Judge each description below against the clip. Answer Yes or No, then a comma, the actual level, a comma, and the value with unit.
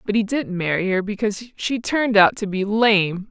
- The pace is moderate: No, fast, 220 wpm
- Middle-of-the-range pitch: No, high, 210 Hz